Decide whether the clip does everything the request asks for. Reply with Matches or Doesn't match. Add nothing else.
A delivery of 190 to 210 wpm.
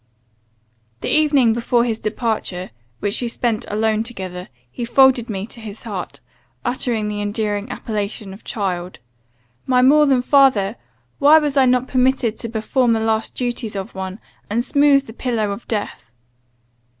Doesn't match